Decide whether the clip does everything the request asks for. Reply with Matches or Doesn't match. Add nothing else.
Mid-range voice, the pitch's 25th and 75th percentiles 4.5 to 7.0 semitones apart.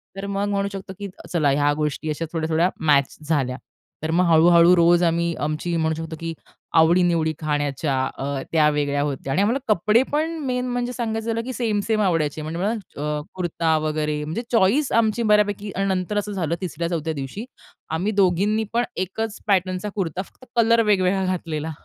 Matches